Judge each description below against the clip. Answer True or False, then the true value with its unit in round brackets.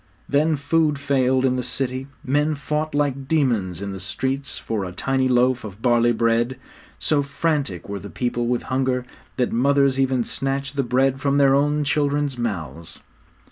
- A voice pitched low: True (130 Hz)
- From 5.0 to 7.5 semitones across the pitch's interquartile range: False (2.9 semitones)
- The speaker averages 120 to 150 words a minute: False (170 wpm)